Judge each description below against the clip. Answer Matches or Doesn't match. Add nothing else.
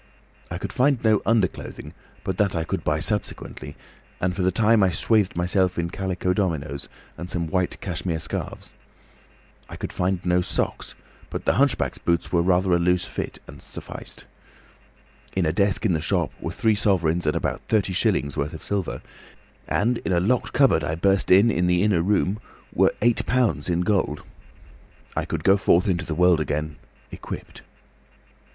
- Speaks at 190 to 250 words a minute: Doesn't match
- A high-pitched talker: Doesn't match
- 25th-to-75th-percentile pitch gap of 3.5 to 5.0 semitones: Doesn't match